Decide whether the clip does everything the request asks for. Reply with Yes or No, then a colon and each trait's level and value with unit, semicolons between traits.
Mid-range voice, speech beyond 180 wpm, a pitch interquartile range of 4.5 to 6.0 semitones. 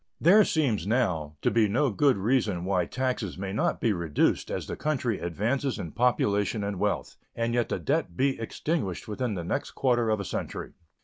No: low, 110 Hz; average, 190 wpm; average, 5.0 semitones